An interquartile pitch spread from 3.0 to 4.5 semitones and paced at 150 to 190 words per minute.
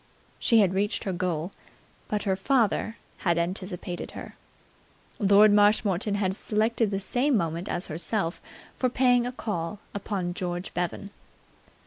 No: average, 3.4 semitones; slow, 135 wpm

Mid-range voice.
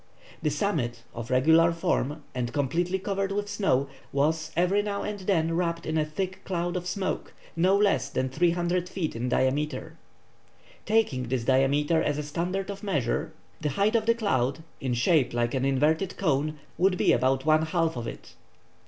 Yes: medium, 160 Hz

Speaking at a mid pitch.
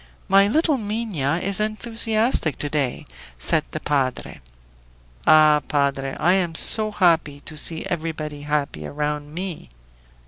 Yes: medium, 160 Hz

